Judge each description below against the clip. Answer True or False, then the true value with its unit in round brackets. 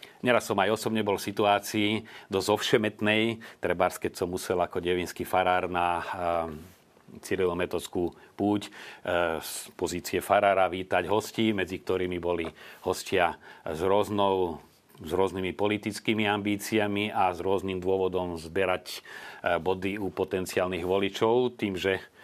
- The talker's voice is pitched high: False (95 Hz)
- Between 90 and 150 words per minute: True (120 wpm)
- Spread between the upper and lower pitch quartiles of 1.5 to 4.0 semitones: True (2.5 semitones)